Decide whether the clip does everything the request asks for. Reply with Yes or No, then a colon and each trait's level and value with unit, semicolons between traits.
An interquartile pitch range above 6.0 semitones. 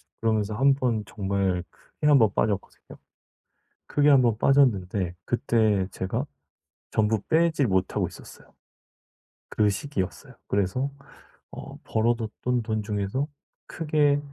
No: wide, 5.4 semitones